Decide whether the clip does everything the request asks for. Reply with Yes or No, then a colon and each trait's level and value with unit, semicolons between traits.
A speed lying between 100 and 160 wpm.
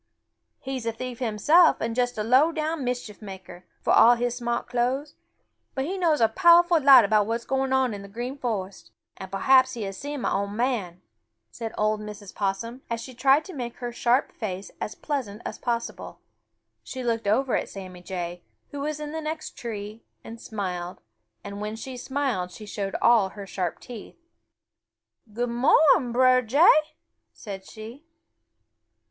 No: average, 175 wpm